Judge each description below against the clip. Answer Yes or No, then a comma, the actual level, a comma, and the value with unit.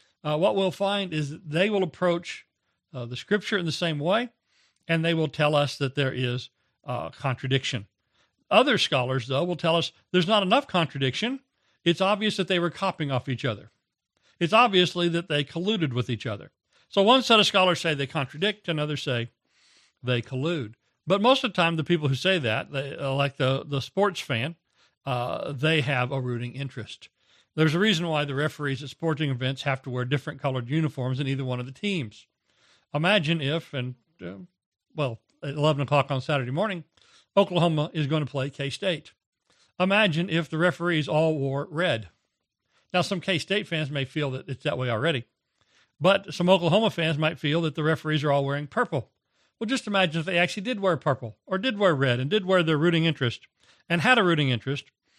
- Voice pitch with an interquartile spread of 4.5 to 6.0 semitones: Yes, average, 4.9 semitones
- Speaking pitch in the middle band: Yes, medium, 155 Hz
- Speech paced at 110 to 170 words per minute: No, average, 195 wpm